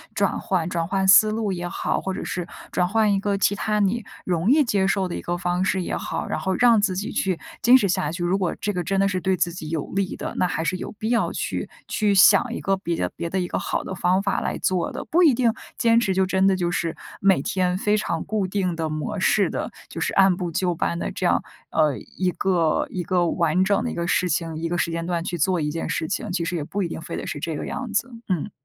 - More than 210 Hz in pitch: No, medium, 185 Hz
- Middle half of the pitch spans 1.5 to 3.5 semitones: Yes, average, 2.8 semitones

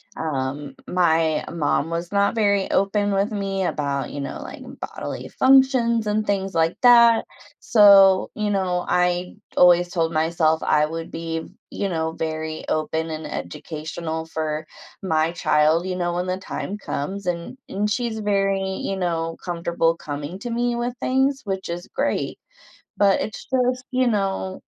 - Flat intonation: No, average, 4.1 semitones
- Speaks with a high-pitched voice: No, medium, 180 Hz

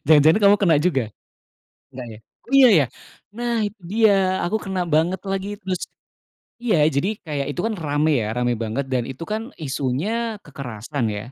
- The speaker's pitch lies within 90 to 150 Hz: No, medium, 165 Hz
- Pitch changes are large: Yes, wide, 7.1 semitones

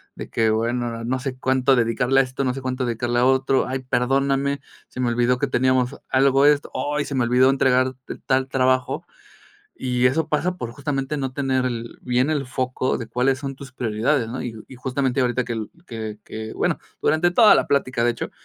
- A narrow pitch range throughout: Yes, narrow, 1.7 semitones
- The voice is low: Yes, low, 130 Hz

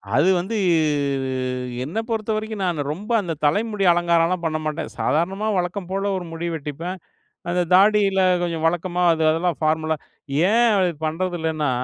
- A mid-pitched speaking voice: Yes, medium, 175 Hz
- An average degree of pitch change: Yes, average, 3.4 semitones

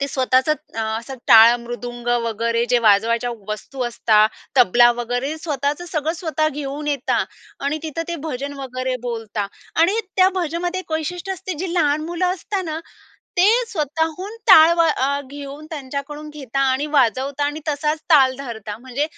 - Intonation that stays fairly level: No, average, 4.5 semitones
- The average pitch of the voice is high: Yes, very high, 280 Hz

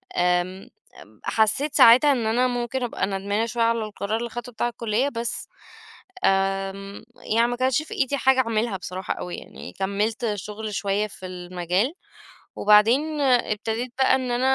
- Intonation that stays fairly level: No, average, 3.7 semitones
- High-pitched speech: Yes, high, 225 Hz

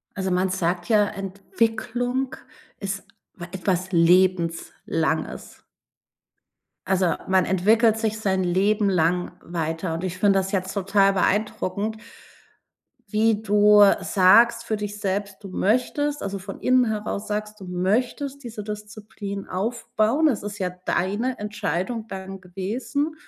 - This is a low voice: No, high, 200 Hz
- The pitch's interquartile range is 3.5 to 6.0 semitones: No, average, 2.8 semitones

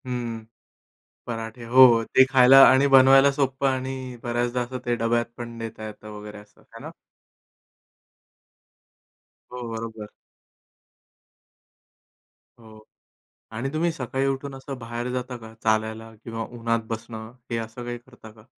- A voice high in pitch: No, low, 120 Hz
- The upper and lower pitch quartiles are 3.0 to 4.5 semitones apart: No, narrow, 2.6 semitones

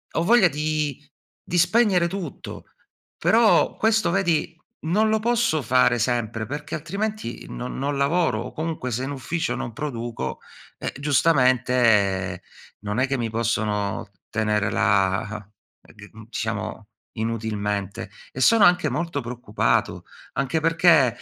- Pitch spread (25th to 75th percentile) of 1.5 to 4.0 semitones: No, wide, 7.2 semitones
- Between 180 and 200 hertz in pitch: No, low, 130 Hz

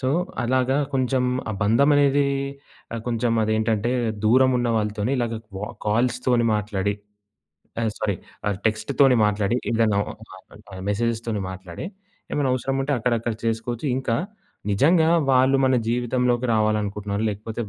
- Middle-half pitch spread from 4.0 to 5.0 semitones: No, average, 3.3 semitones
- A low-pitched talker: Yes, low, 115 Hz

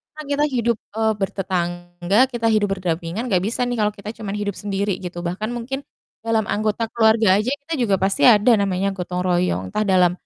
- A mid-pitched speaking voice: No, high, 205 Hz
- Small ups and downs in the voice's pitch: No, average, 3.5 semitones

